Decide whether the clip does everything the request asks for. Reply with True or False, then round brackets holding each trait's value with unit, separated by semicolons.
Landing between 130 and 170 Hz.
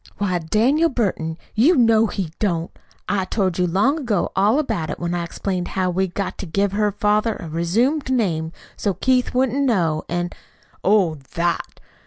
False (200 Hz)